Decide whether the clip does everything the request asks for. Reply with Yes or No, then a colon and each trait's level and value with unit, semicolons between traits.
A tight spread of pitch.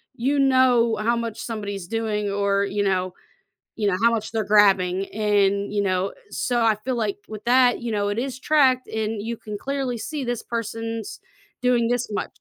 No: average, 3.0 semitones